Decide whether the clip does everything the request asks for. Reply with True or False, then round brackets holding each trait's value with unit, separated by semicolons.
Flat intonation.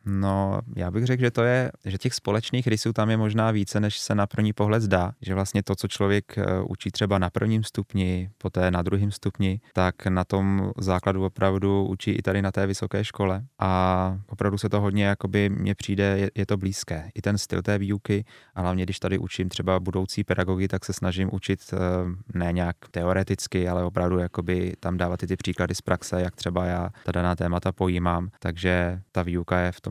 True (2.2 semitones)